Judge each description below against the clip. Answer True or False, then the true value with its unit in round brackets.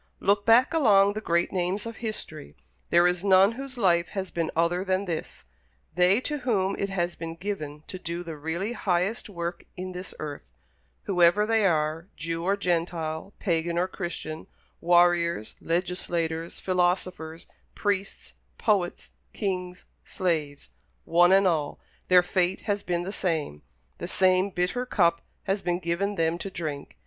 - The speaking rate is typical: True (155 wpm)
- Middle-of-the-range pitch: True (180 Hz)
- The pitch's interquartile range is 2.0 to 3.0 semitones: True (2.7 semitones)